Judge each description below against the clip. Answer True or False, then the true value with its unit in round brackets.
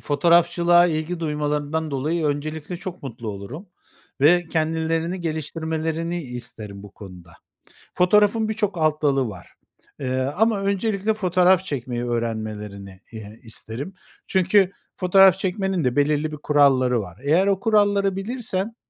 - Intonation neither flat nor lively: False (6.2 semitones)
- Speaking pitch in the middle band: True (160 Hz)